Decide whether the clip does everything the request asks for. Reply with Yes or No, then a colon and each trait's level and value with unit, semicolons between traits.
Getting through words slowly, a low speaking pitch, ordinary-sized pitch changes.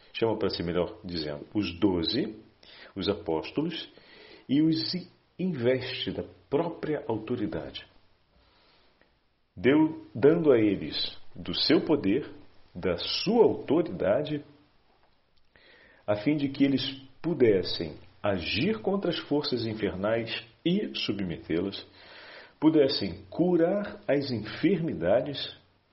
No: slow, 95 wpm; low, 125 Hz; wide, 7.7 semitones